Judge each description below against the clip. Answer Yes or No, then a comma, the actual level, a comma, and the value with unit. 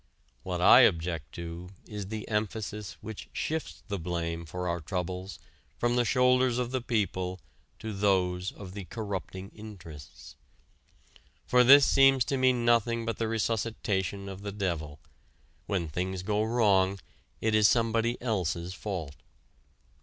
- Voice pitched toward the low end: Yes, low, 100 Hz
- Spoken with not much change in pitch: No, average, 4.1 semitones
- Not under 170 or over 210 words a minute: No, average, 140 wpm